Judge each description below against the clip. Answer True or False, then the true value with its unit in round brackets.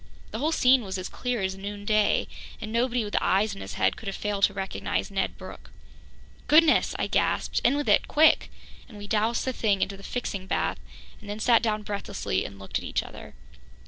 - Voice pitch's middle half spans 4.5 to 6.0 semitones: False (3.4 semitones)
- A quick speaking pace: True (210 wpm)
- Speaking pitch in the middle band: False (210 Hz)